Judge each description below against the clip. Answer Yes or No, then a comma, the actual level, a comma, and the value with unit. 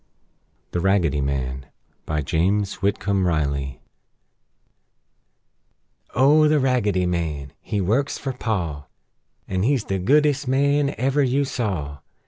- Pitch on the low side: Yes, low, 100 Hz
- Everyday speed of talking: No, slow, 110 wpm